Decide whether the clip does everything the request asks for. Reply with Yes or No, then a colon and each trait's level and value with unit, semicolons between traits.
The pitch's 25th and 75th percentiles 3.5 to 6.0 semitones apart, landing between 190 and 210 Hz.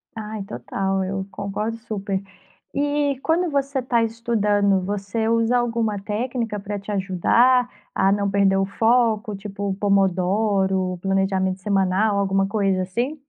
No: average, 3.0 semitones; high, 205 Hz